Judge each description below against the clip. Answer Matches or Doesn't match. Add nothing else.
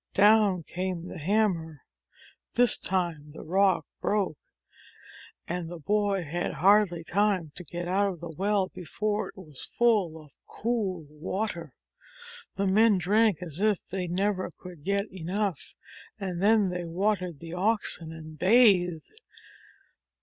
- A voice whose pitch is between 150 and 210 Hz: Matches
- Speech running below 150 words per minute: Matches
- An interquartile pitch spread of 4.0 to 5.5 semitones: Doesn't match